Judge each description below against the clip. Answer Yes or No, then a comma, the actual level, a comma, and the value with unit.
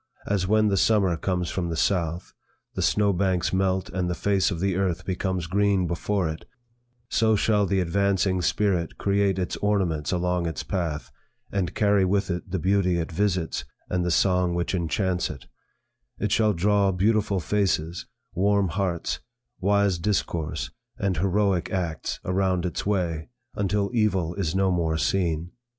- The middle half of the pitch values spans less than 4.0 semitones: Yes, narrow, 2.4 semitones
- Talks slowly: No, average, 160 wpm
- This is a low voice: Yes, very low, 95 Hz